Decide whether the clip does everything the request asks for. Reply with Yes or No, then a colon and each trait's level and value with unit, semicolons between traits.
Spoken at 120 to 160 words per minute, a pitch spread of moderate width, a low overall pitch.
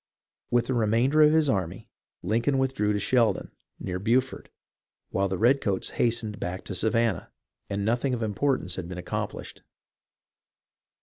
Yes: average, 140 wpm; average, 4.7 semitones; low, 115 Hz